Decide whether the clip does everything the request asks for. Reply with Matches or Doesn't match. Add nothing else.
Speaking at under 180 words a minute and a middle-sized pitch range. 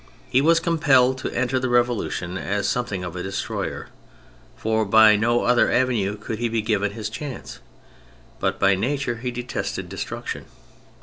Matches